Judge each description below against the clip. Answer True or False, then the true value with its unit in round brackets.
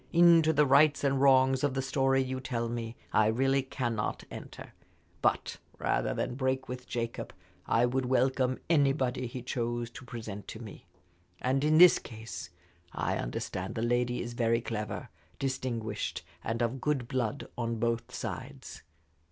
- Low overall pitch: True (125 Hz)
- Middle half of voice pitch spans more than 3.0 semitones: False (2.4 semitones)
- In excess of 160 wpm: False (155 wpm)